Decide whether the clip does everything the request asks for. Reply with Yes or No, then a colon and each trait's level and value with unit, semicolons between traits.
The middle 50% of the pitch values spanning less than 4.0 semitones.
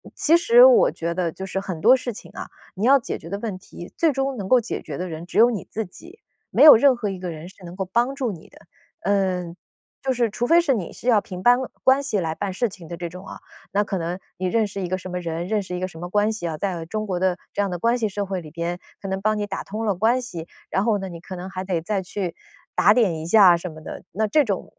No: average, 4.3 semitones